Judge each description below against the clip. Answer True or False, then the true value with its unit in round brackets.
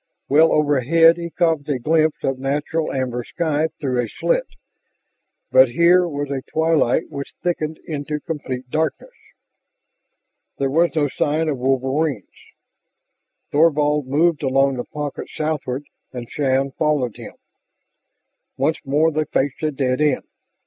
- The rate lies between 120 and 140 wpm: True (135 wpm)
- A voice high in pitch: False (145 Hz)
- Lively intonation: False (3.0 semitones)